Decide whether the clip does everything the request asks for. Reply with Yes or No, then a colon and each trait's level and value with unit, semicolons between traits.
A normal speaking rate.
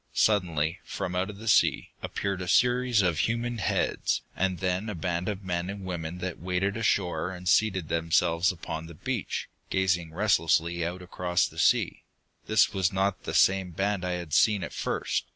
Yes: average, 180 wpm